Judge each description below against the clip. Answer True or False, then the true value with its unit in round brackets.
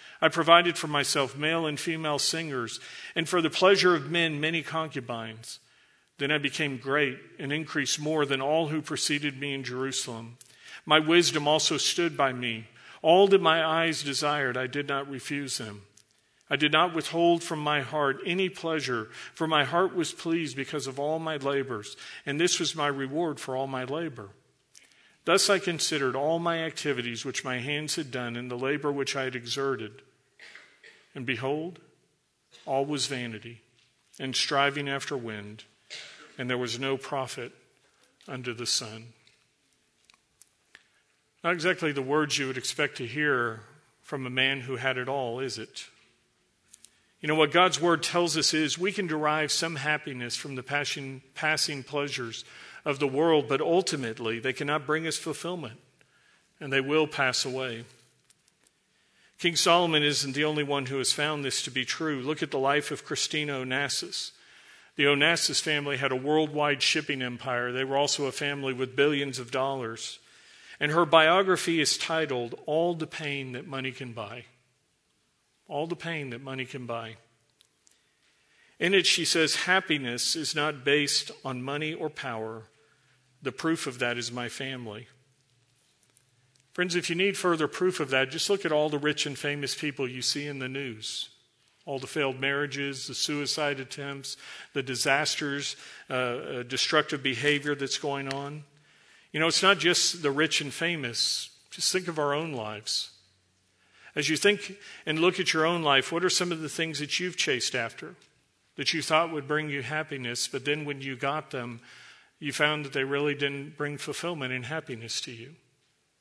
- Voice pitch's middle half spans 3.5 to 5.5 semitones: False (3.1 semitones)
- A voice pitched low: False (145 Hz)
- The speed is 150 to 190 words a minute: True (170 wpm)